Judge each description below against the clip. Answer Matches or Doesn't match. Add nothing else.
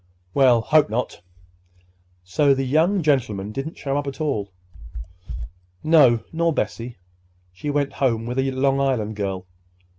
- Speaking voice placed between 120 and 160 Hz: Matches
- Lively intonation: Doesn't match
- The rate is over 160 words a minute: Doesn't match